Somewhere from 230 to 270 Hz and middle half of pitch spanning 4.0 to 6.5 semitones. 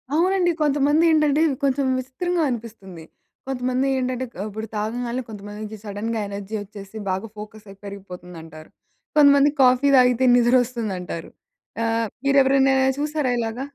Yes: high, 240 Hz; average, 4.7 semitones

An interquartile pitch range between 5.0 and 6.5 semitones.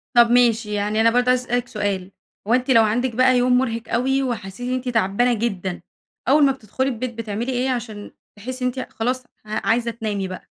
No: average, 2.8 semitones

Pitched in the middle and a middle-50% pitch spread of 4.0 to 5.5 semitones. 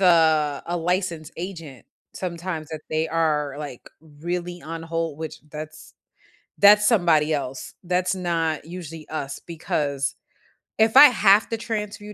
No: medium, 165 Hz; average, 3.0 semitones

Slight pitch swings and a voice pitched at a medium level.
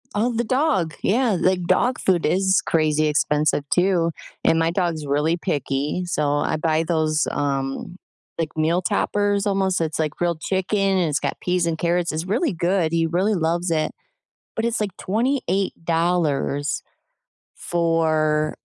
No: average, 3.5 semitones; medium, 170 Hz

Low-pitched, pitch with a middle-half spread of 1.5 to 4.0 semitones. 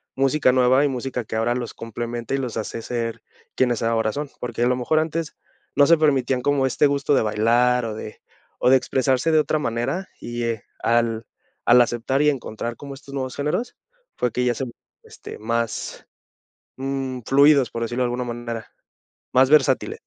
Yes: low, 125 Hz; average, 2.8 semitones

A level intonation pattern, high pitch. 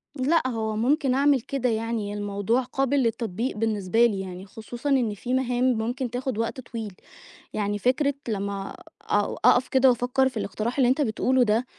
No: average, 3.4 semitones; high, 235 Hz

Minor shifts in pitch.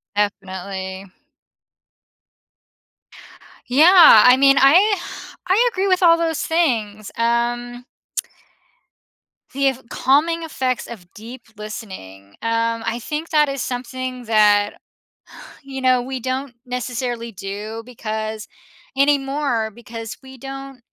No: average, 3.9 semitones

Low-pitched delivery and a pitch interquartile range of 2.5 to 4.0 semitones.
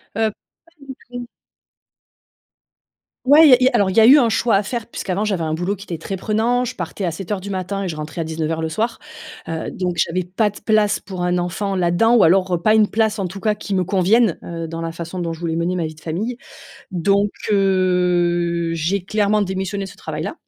No: high, 190 Hz; average, 3.7 semitones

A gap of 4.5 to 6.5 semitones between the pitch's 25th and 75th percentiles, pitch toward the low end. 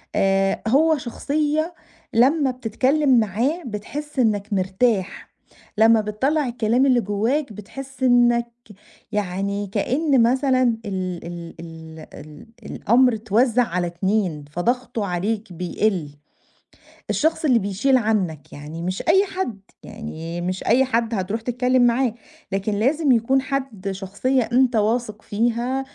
No: average, 4.9 semitones; high, 225 Hz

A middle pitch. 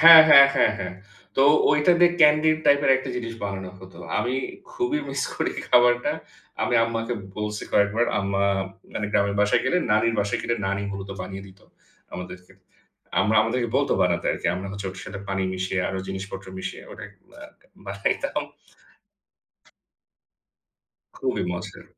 No: low, 105 Hz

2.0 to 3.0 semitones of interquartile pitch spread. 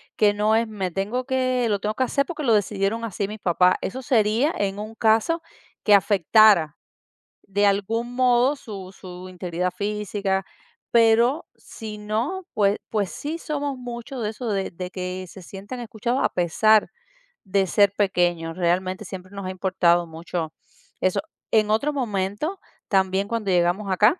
No: average, 3.7 semitones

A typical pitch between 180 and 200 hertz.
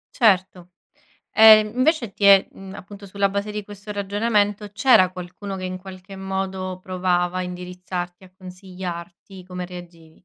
Yes: high, 190 Hz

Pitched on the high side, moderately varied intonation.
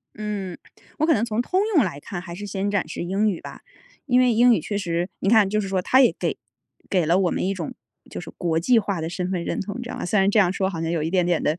Yes: high, 195 Hz; average, 3.5 semitones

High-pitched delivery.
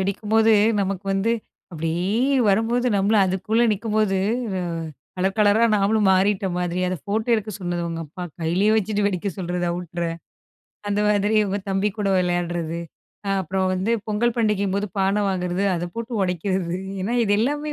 Yes: high, 195 Hz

